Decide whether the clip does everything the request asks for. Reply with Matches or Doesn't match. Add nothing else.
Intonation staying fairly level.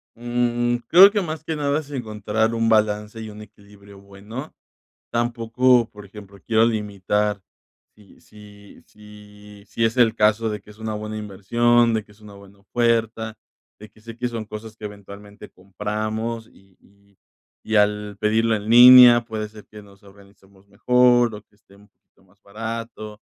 Matches